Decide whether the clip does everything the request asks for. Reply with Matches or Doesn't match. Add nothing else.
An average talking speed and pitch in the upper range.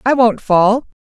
Matches